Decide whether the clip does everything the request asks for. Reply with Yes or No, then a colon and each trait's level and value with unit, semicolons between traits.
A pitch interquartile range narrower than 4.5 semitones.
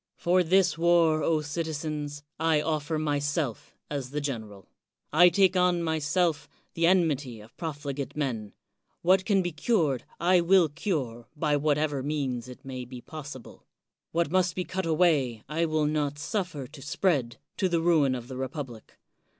Yes: average, 3.6 semitones